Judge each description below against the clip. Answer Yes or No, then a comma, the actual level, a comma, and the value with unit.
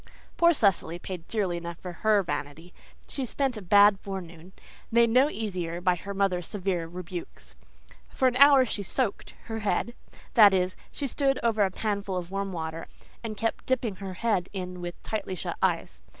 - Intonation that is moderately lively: Yes, average, 4.1 semitones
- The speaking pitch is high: Yes, high, 195 Hz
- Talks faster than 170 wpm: Yes, average, 180 wpm